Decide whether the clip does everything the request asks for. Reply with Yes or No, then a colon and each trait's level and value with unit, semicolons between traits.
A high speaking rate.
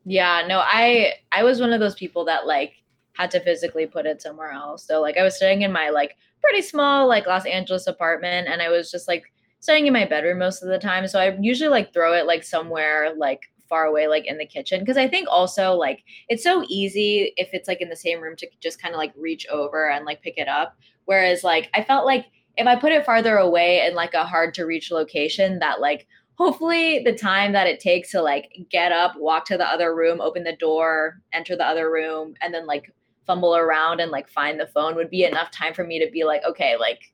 Yes: fast, 240 wpm